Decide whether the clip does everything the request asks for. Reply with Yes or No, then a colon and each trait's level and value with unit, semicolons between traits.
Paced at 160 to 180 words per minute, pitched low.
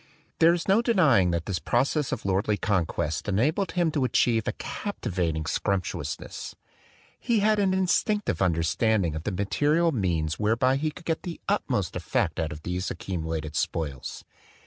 Yes: average, 165 wpm; low, 105 Hz